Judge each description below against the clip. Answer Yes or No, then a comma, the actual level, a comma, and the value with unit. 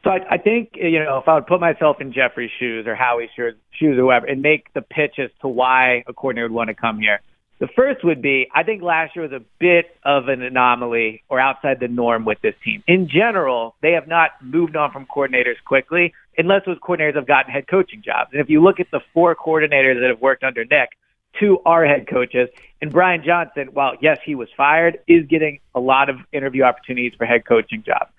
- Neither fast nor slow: No, fast, 230 wpm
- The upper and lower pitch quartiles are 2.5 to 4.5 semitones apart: No, average, 4.9 semitones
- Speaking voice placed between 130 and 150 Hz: Yes, medium, 140 Hz